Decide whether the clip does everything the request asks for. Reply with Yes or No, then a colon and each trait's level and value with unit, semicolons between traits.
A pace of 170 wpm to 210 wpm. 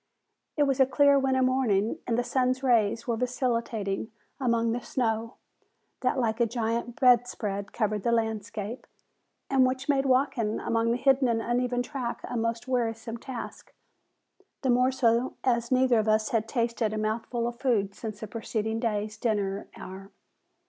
No: average, 160 wpm